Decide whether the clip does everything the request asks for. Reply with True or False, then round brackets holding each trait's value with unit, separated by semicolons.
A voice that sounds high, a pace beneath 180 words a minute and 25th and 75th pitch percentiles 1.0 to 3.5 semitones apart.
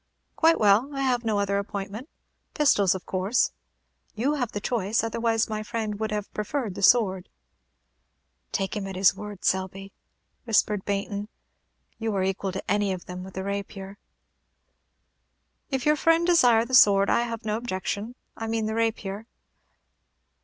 True (210 Hz; 160 wpm; 2.9 semitones)